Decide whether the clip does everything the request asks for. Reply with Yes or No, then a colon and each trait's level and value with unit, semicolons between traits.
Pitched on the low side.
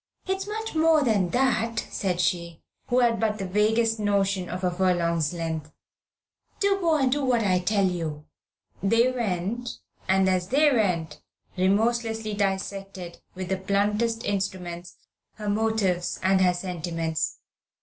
No: high, 200 Hz